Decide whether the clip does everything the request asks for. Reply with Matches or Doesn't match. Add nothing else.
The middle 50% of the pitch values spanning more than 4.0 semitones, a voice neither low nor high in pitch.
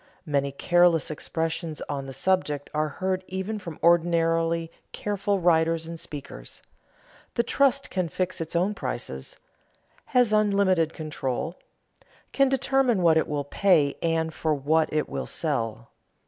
Doesn't match